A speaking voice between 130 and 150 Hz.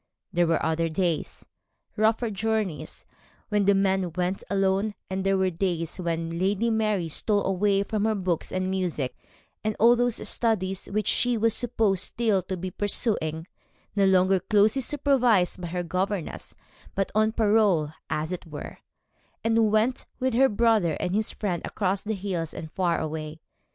No: high, 195 Hz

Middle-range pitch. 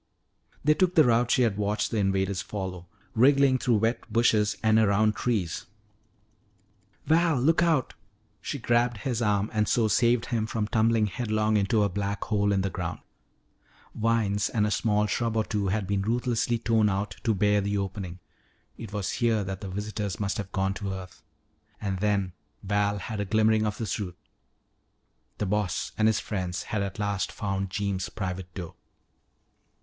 No: low, 105 Hz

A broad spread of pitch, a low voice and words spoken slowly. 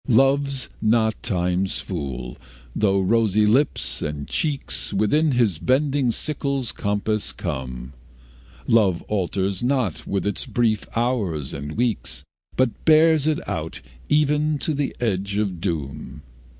Yes: wide, 6.7 semitones; low, 110 Hz; slow, 125 wpm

